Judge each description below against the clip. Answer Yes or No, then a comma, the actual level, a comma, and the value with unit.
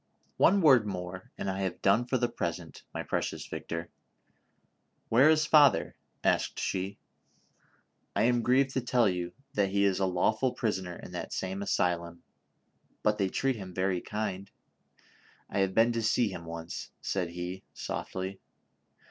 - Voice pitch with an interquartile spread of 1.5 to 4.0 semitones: No, average, 4.4 semitones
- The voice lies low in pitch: Yes, low, 100 Hz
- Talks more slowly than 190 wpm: Yes, average, 165 wpm